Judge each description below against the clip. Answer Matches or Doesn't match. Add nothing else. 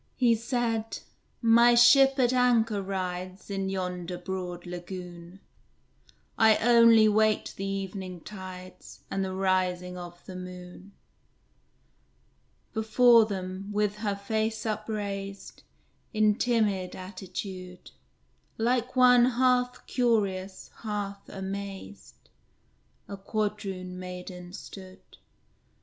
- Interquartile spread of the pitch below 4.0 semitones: Matches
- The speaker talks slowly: Matches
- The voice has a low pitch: Doesn't match